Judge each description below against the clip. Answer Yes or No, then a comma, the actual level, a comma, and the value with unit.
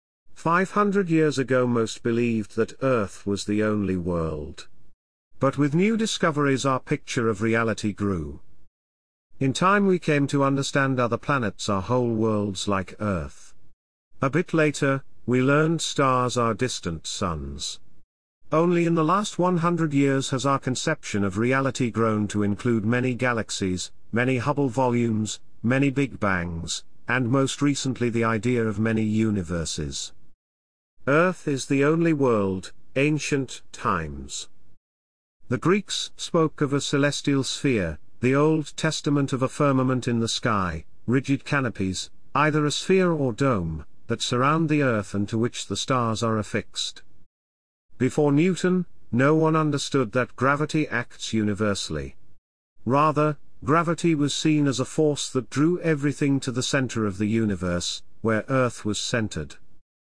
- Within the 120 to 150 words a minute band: Yes, average, 140 wpm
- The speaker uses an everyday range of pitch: No, wide, 6.2 semitones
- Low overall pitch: Yes, low, 125 Hz